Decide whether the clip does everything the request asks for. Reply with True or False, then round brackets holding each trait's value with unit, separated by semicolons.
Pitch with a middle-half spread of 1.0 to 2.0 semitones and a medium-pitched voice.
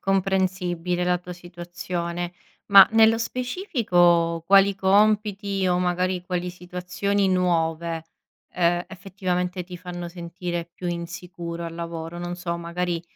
True (1.6 semitones; 180 Hz)